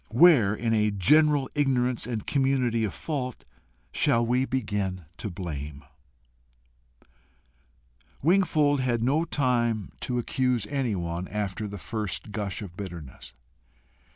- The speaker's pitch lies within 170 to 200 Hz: No, low, 115 Hz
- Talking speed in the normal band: No, slow, 115 wpm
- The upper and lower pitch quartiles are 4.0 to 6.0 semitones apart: Yes, average, 4.9 semitones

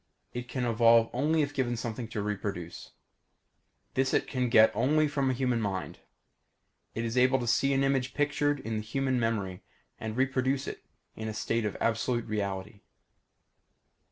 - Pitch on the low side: Yes, low, 120 Hz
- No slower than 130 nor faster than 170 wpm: Yes, average, 165 wpm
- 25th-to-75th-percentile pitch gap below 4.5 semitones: Yes, average, 3.3 semitones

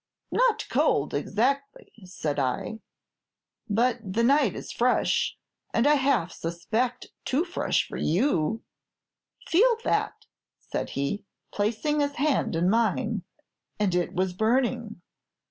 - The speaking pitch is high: Yes, high, 230 Hz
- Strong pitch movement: Yes, wide, 7.1 semitones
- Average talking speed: No, slow, 120 wpm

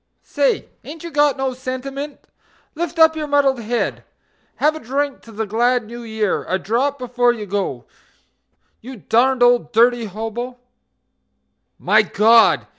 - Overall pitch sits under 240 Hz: No, high, 245 Hz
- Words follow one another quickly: No, average, 145 wpm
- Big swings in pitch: No, average, 4.0 semitones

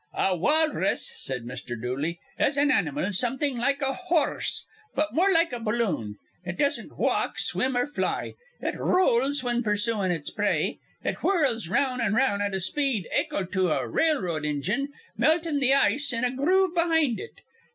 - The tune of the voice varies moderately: No, wide, 7.4 semitones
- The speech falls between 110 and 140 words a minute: No, average, 175 wpm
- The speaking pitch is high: Yes, very high, 255 Hz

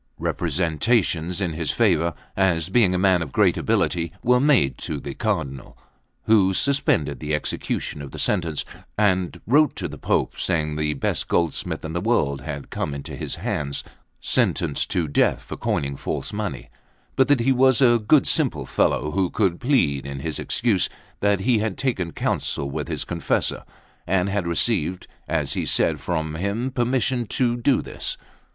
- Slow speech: No, average, 170 wpm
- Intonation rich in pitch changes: Yes, wide, 7.2 semitones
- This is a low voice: Yes, very low, 90 Hz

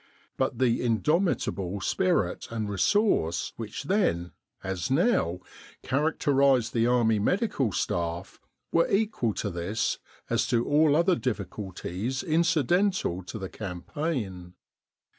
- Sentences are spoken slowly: Yes, slow, 120 wpm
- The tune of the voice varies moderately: No, wide, 8.8 semitones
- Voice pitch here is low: Yes, low, 120 Hz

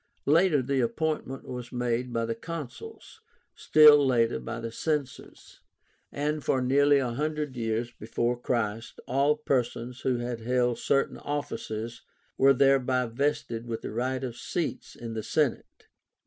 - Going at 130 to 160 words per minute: Yes, average, 145 wpm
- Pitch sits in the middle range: No, low, 125 Hz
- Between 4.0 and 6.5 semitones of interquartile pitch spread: No, average, 3.3 semitones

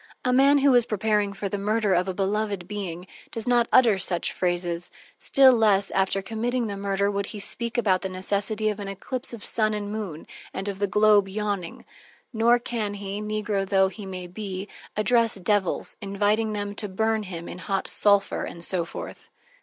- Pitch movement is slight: Yes, narrow, 2.2 semitones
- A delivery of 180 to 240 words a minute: Yes, average, 190 wpm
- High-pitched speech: Yes, high, 205 Hz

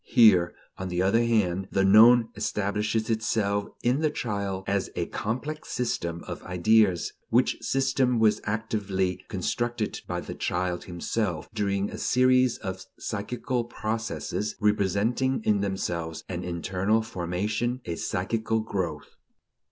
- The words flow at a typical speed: No, slow, 130 wpm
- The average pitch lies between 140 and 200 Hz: No, low, 105 Hz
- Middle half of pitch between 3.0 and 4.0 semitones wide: Yes, average, 3.5 semitones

